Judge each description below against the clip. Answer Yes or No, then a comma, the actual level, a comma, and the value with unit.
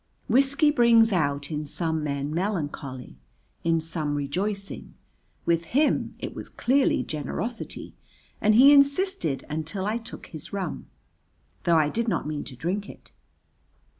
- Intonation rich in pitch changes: Yes, wide, 7.3 semitones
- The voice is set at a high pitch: No, medium, 175 Hz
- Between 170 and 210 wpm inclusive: No, slow, 135 wpm